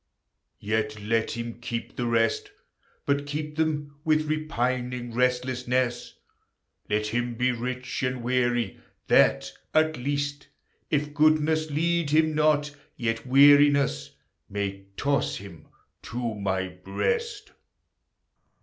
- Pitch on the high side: No, low, 125 Hz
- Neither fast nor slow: No, slow, 110 wpm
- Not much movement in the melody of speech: No, average, 4.3 semitones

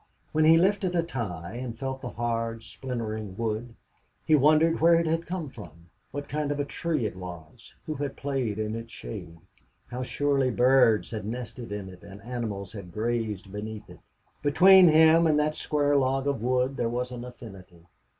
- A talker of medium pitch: No, low, 125 Hz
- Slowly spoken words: No, average, 185 wpm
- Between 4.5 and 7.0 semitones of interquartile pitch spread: Yes, average, 5.2 semitones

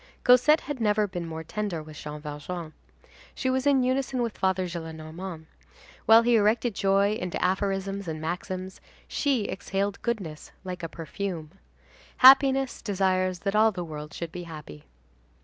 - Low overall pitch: No, high, 190 Hz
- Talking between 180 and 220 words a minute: No, average, 150 wpm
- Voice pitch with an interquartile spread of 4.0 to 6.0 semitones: Yes, average, 5.1 semitones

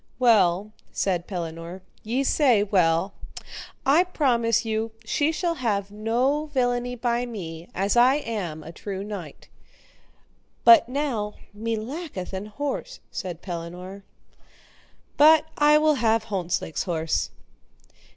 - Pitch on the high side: Yes, high, 220 Hz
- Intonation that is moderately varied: No, wide, 5.7 semitones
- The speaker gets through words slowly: Yes, slow, 115 wpm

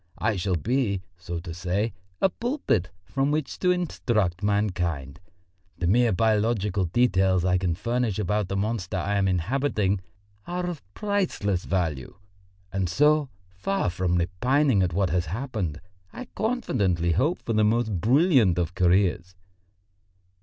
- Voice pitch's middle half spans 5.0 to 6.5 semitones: Yes, wide, 5.6 semitones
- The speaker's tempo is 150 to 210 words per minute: No, average, 140 wpm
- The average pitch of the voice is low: Yes, low, 100 Hz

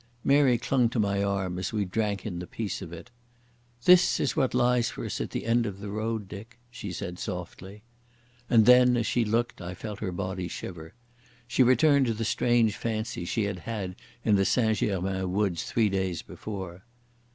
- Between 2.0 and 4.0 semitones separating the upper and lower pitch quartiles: Yes, average, 3.7 semitones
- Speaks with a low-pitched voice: Yes, low, 105 Hz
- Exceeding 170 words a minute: Yes, average, 195 wpm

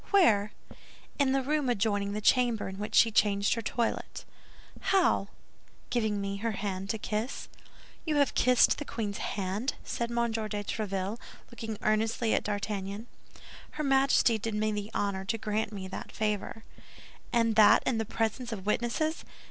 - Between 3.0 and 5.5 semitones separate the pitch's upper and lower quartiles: No, narrow, 2.6 semitones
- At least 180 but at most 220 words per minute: No, average, 160 wpm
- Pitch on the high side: Yes, high, 220 Hz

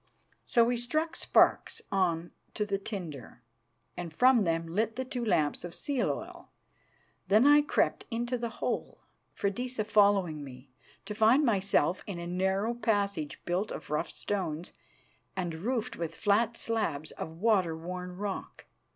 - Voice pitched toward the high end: Yes, high, 200 Hz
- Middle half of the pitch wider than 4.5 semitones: Yes, average, 5.2 semitones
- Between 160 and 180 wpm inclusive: No, average, 150 wpm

